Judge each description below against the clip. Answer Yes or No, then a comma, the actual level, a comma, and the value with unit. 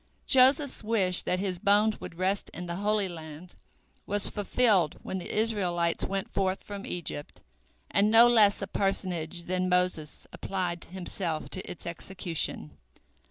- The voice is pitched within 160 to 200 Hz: Yes, medium, 185 Hz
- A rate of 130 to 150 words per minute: Yes, average, 145 wpm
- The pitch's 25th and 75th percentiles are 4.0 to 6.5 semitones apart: No, average, 3.0 semitones